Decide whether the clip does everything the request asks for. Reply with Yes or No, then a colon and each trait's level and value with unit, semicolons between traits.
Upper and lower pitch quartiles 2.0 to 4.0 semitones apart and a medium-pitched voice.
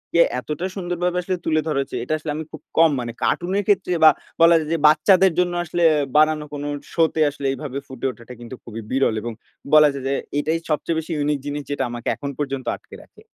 Yes: average, 3.5 semitones; medium, 155 Hz